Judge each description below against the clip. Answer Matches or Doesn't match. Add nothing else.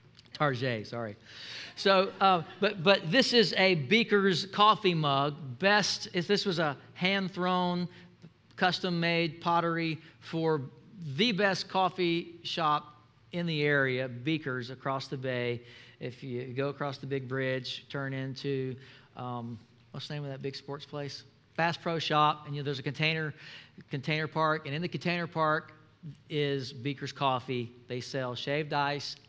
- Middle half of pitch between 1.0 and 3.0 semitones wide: Doesn't match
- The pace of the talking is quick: Doesn't match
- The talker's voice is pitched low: Doesn't match